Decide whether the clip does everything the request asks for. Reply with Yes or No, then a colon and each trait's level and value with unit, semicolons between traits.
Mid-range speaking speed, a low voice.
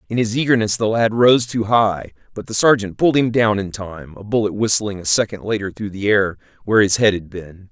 No: fast, 235 wpm; low, 105 Hz